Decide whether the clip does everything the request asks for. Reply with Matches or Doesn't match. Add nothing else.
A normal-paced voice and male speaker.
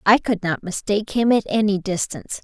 Doesn't match